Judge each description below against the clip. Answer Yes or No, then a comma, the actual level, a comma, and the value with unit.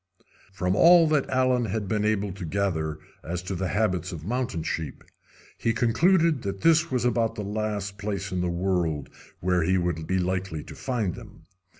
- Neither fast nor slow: Yes, average, 185 wpm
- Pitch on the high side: No, low, 100 Hz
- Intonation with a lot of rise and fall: No, average, 4.5 semitones